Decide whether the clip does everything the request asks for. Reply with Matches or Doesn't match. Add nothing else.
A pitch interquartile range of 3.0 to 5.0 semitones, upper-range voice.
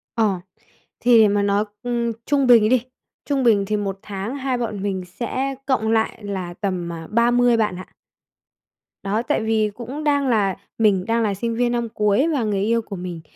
Matches